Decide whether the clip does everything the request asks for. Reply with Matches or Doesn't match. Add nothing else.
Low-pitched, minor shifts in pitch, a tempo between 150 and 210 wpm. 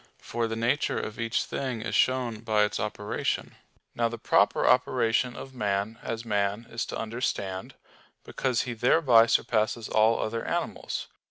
Matches